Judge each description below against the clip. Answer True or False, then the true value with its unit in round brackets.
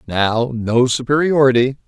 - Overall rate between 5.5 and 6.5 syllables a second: False (4.4 syllables/s)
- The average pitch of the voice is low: True (125 Hz)